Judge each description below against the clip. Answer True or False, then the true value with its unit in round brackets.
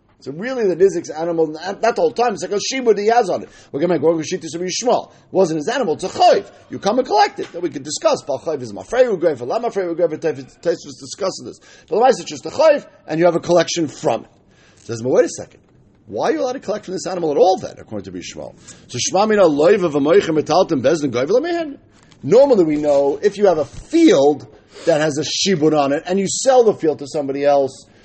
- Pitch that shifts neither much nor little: False (7.7 semitones)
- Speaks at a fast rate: True (245 wpm)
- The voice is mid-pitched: True (180 Hz)